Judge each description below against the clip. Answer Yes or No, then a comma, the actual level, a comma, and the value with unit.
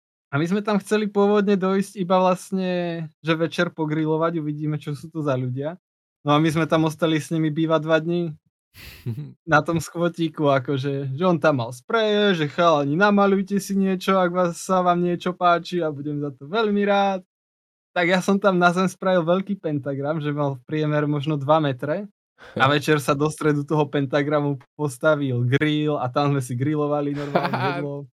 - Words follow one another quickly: Yes, fast, 190 wpm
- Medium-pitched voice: Yes, medium, 160 Hz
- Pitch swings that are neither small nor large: Yes, average, 3.7 semitones